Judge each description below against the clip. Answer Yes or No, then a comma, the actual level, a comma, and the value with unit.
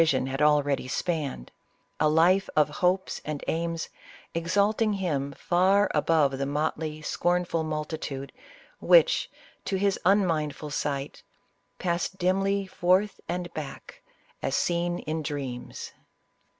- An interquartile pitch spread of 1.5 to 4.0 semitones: Yes, average, 3.7 semitones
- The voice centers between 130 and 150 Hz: No, medium, 165 Hz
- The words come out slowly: Yes, slow, 125 wpm